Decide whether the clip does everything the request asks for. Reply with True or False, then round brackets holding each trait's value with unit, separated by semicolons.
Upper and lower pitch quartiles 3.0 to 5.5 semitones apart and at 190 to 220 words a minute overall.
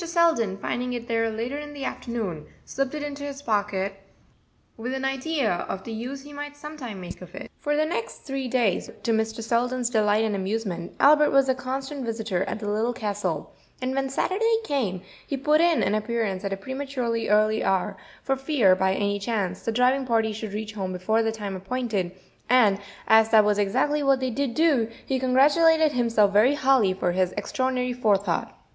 True (4.7 semitones; 195 wpm)